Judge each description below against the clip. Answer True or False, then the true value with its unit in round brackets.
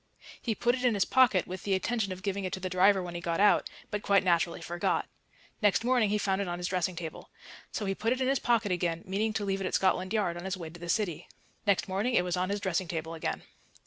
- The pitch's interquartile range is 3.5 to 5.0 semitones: False (2.9 semitones)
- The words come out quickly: True (270 wpm)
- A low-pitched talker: False (190 Hz)